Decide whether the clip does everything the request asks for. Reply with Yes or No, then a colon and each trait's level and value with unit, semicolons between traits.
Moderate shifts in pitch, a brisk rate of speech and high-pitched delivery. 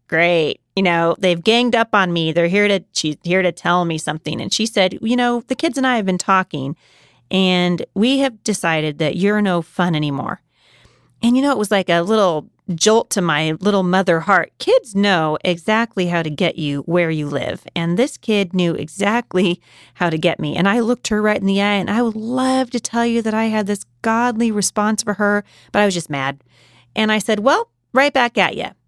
Yes: average, 4.6 semitones; fast, 220 wpm; high, 195 Hz